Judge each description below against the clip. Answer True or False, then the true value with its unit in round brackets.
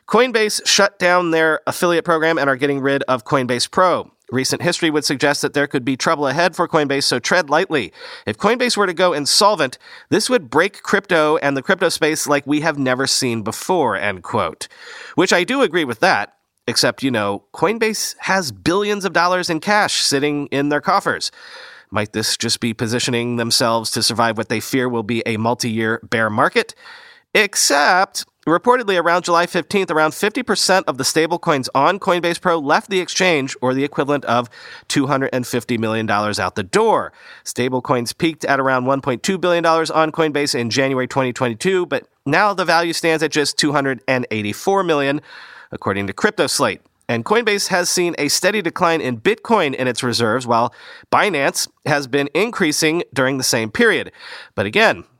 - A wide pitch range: True (5.7 semitones)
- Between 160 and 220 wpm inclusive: True (170 wpm)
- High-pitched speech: False (145 Hz)